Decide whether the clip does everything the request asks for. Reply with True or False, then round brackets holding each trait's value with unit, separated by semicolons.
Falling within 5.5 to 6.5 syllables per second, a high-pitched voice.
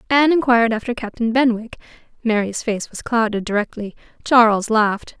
True (5.7 syllables/s; 230 Hz)